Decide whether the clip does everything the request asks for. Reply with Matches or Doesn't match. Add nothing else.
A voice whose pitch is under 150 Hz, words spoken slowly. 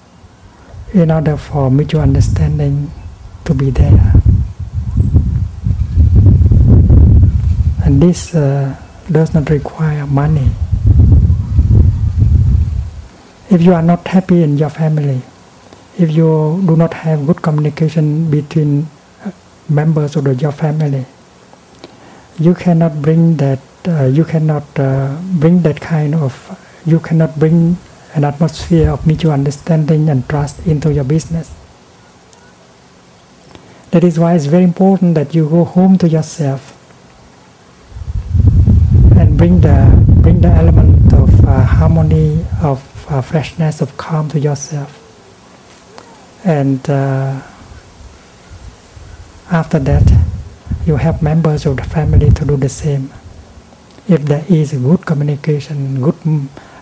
Matches